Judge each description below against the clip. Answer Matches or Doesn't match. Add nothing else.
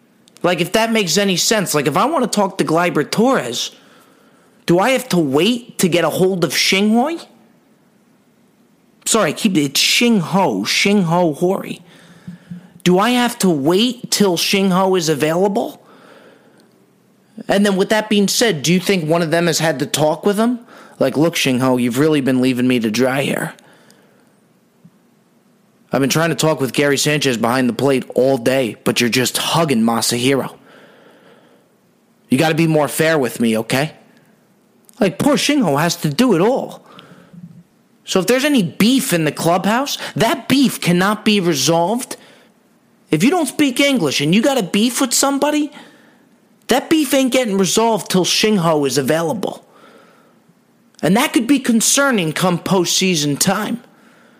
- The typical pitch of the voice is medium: Doesn't match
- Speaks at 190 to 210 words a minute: Doesn't match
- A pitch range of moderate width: Doesn't match